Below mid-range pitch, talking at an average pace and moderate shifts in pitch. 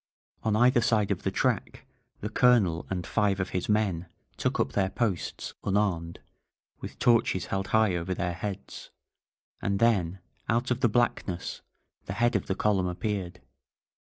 Yes: low, 100 Hz; average, 160 wpm; average, 3.4 semitones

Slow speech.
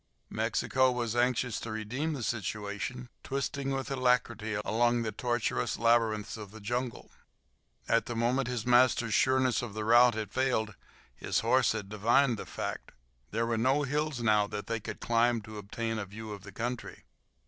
No: average, 170 wpm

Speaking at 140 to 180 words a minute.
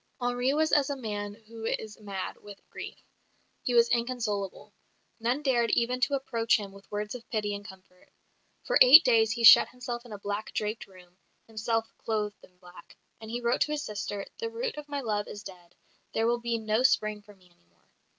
No: fast, 205 wpm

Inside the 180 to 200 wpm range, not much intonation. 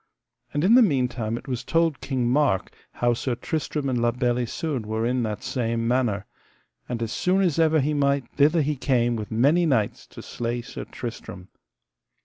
No: average, 185 wpm; average, 3.9 semitones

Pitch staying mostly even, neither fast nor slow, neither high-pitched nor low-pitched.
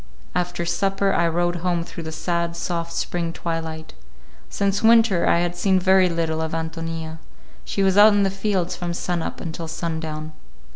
Yes: narrow, 2.3 semitones; average, 180 wpm; medium, 170 Hz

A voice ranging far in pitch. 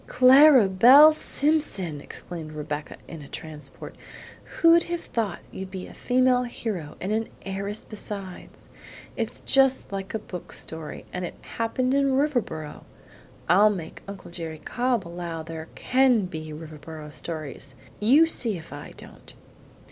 Yes: wide, 7.8 semitones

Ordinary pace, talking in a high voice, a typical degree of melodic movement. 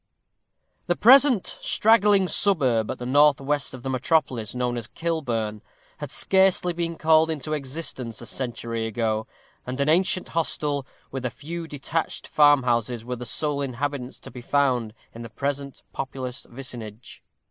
No: average, 155 wpm; low, 135 Hz; average, 4.8 semitones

